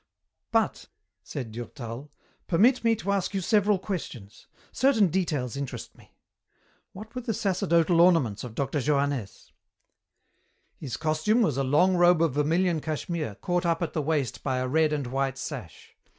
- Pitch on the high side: No, medium, 155 Hz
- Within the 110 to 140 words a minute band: No, average, 155 wpm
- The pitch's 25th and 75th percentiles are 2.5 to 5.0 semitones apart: No, wide, 5.4 semitones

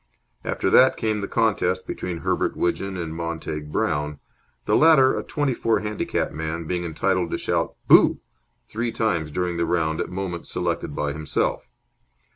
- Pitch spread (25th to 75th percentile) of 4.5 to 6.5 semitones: Yes, average, 5.1 semitones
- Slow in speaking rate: No, average, 160 wpm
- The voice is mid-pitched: No, very low, 90 Hz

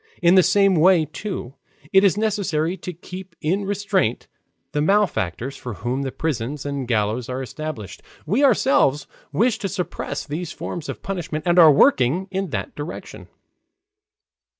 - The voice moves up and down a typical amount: No, wide, 5.9 semitones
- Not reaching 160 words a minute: Yes, average, 150 wpm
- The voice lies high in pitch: No, medium, 165 Hz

